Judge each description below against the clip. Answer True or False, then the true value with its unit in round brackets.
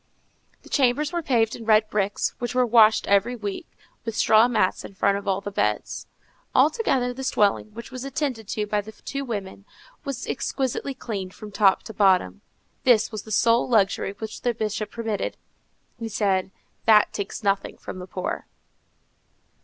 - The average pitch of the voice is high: True (220 Hz)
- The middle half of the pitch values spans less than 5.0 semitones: True (3.5 semitones)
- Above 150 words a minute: True (170 wpm)